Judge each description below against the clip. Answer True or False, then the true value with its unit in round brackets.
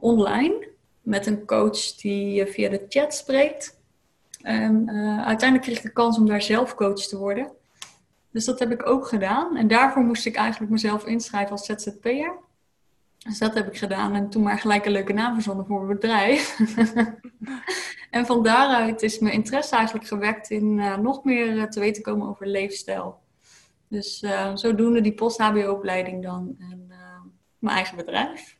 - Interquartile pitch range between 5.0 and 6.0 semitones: False (2.6 semitones)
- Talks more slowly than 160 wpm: False (170 wpm)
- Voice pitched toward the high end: True (215 Hz)